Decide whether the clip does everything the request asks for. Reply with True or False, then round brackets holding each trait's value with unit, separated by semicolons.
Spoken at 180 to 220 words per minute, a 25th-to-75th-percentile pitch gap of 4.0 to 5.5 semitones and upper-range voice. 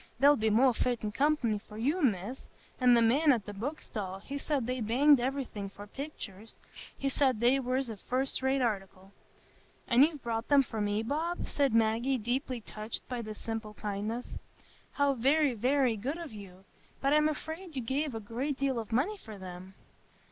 True (185 wpm; 4.3 semitones; 245 Hz)